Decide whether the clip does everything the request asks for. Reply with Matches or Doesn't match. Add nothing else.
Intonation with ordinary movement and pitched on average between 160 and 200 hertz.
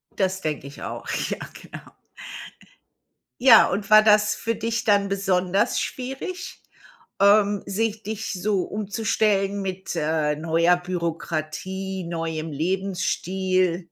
Matches